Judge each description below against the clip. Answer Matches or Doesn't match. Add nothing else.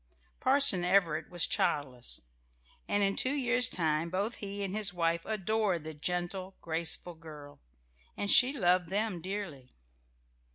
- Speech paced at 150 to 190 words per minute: Doesn't match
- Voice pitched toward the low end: Doesn't match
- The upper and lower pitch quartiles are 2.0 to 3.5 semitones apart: Doesn't match